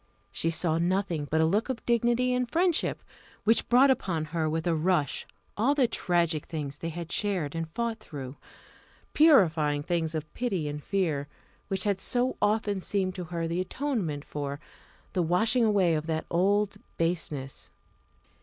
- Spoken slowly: No, average, 165 wpm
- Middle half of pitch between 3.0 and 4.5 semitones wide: No, average, 5.3 semitones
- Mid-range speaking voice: Yes, medium, 175 Hz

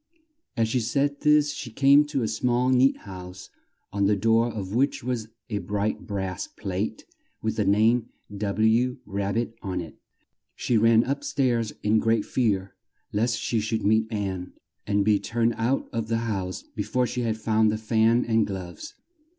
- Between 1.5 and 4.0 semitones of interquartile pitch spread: Yes, average, 2.8 semitones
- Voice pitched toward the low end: Yes, low, 110 Hz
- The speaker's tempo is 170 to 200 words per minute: Yes, average, 175 wpm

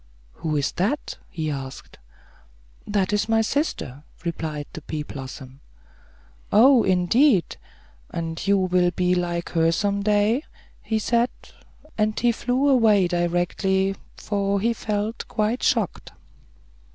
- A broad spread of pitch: No, average, 4.6 semitones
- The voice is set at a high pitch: Yes, high, 195 Hz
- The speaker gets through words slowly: Yes, slow, 125 wpm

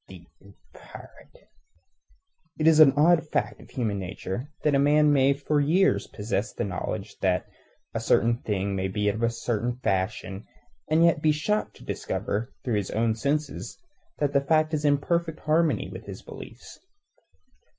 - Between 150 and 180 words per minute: Yes, average, 170 wpm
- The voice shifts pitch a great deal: Yes, wide, 6.6 semitones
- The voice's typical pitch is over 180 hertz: No, low, 135 Hz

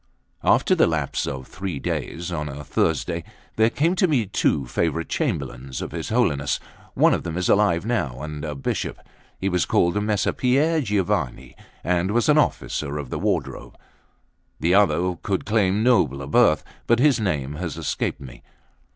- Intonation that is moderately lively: No, wide, 6.2 semitones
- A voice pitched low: Yes, very low, 85 Hz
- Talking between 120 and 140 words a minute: No, average, 170 wpm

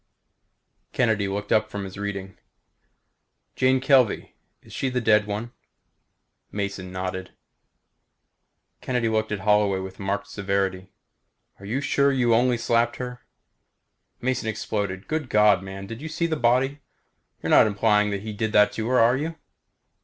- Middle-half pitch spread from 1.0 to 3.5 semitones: No, average, 3.9 semitones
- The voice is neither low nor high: No, low, 110 Hz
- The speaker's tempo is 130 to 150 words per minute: Yes, average, 145 wpm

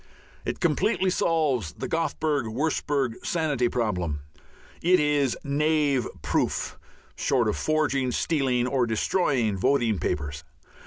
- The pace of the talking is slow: Yes, slow, 110 wpm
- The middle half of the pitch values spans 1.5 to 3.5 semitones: No, average, 4.7 semitones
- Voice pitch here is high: No, low, 135 Hz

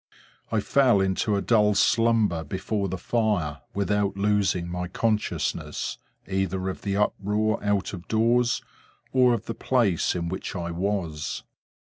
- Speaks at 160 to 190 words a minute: No, average, 140 wpm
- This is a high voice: No, low, 100 Hz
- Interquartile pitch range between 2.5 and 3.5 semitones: Yes, average, 2.8 semitones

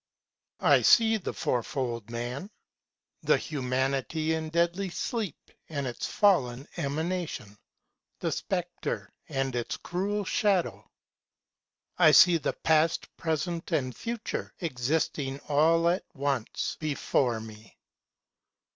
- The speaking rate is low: Yes, slow, 95 wpm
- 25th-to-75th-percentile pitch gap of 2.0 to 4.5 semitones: No, average, 5.3 semitones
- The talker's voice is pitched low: No, medium, 150 Hz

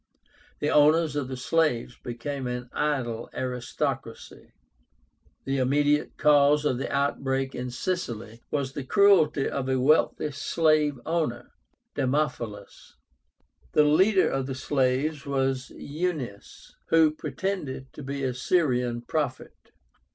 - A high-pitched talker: No, medium, 140 Hz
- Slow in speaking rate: Yes, slow, 120 wpm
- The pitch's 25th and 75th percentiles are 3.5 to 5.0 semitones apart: No, average, 3.0 semitones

